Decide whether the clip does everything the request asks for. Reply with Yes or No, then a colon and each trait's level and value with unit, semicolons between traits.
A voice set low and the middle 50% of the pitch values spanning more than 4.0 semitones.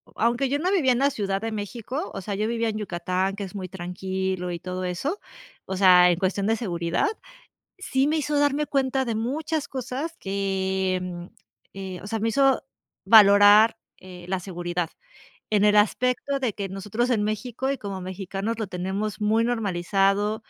No: high, 205 Hz; average, 4.4 semitones